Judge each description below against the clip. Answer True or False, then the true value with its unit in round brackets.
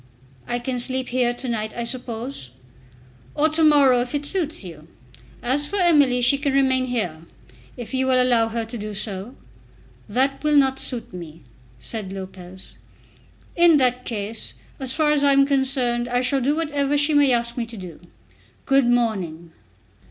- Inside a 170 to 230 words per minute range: True (175 wpm)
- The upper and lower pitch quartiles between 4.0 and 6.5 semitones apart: False (3.6 semitones)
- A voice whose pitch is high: True (250 Hz)